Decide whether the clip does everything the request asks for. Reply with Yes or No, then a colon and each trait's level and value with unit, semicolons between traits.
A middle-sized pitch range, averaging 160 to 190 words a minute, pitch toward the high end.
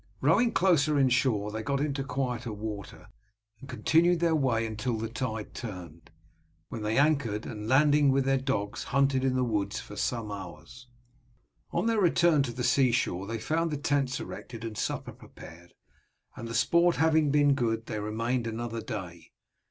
No: average, 4.6 semitones; average, 165 wpm; low, 125 Hz